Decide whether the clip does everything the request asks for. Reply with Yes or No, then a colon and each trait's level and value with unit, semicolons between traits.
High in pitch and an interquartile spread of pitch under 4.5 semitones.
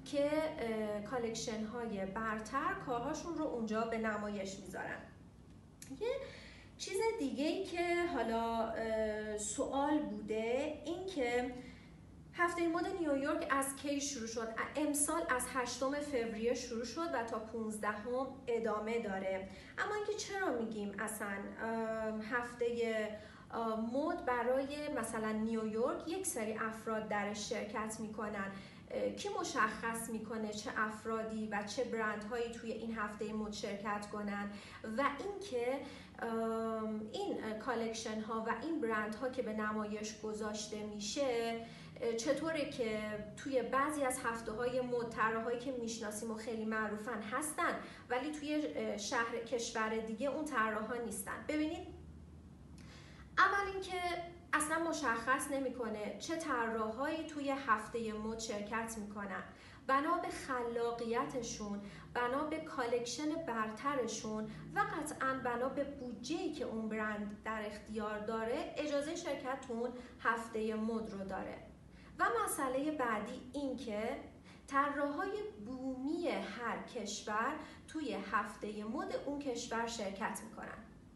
Yes: high, 235 Hz; average, 4.1 semitones